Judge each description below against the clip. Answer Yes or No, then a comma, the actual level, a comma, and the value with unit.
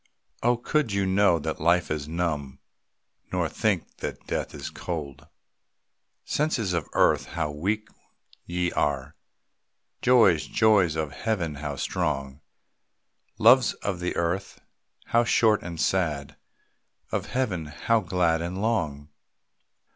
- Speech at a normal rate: No, slow, 125 wpm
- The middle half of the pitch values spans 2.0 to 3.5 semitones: No, average, 4.9 semitones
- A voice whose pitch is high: No, very low, 85 Hz